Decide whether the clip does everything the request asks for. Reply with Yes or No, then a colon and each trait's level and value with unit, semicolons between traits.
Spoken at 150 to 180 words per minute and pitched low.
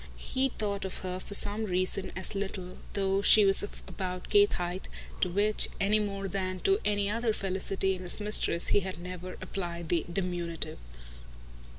No: average, 175 wpm; high, 195 Hz